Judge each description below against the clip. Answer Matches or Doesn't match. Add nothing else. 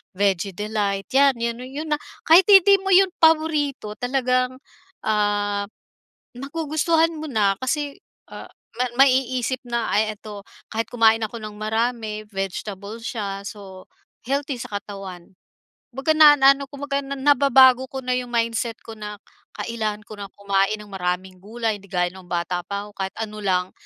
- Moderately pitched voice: Doesn't match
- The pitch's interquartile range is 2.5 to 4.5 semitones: Doesn't match